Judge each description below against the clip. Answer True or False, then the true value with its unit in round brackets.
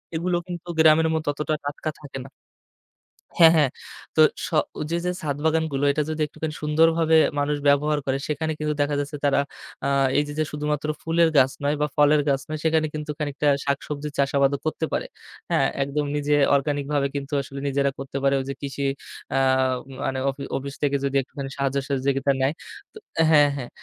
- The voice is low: False (145 Hz)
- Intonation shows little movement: True (1.8 semitones)